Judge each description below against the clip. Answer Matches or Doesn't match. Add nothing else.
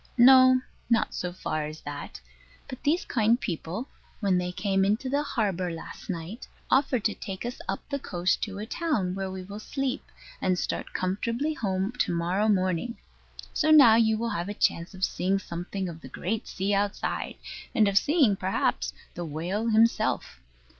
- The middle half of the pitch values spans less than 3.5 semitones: Doesn't match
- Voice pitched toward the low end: Doesn't match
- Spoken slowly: Doesn't match